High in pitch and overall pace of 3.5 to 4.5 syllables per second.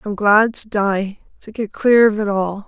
Yes: high, 210 Hz; 4.1 syllables/s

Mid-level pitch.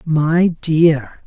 Yes: medium, 165 Hz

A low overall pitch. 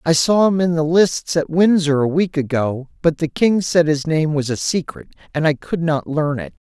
No: medium, 160 Hz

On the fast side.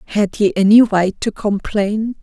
No: average, 160 wpm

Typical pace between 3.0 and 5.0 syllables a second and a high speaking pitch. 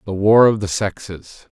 No: 4.4 syllables/s; low, 100 Hz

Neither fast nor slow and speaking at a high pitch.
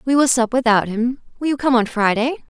No: fast, 230 wpm; high, 245 Hz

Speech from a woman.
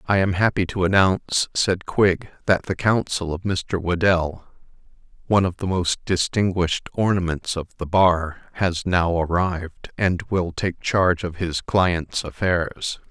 No: male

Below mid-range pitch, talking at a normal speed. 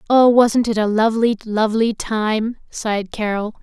No: high, 220 Hz; average, 150 wpm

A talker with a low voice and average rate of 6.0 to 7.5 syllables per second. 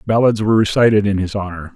Yes: low, 105 Hz; 6.8 syllables/s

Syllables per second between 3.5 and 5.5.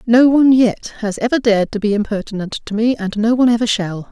No: 6.2 syllables/s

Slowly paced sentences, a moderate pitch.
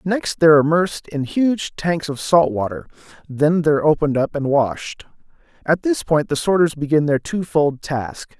No: average, 170 wpm; medium, 155 Hz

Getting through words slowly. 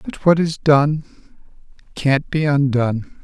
Yes: slow, 130 wpm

